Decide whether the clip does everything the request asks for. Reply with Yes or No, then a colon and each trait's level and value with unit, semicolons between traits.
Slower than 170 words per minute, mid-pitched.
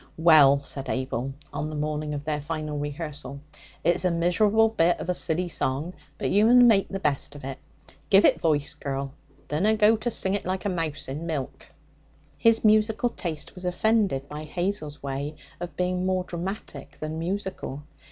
No: average, 180 wpm; medium, 165 Hz